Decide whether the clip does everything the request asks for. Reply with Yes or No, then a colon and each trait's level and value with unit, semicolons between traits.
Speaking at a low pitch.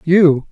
No: medium, 165 Hz